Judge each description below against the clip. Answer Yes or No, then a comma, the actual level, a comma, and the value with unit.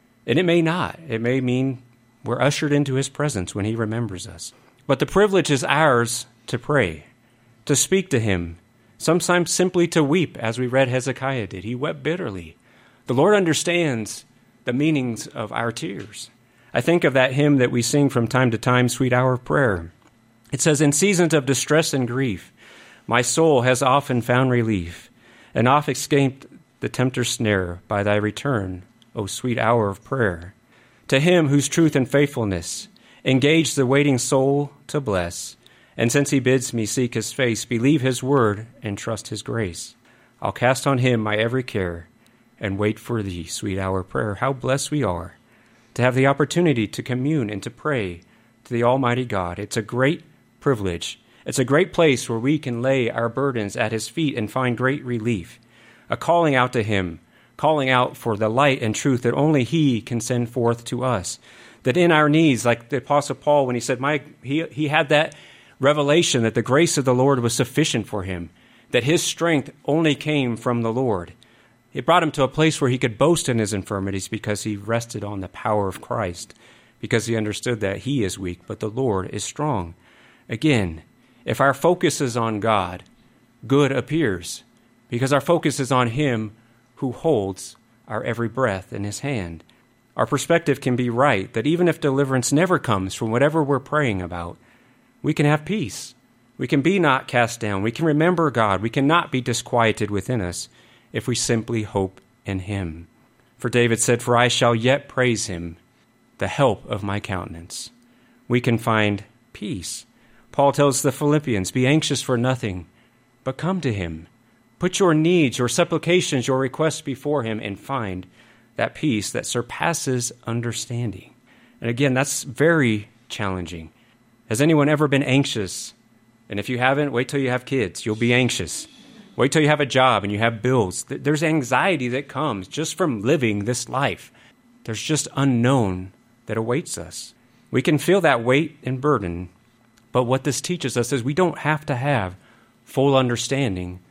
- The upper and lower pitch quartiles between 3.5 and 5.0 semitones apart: Yes, average, 4.1 semitones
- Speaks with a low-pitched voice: Yes, low, 125 Hz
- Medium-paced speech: Yes, average, 180 wpm